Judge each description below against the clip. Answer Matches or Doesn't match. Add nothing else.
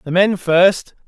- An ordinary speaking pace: Matches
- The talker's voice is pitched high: Doesn't match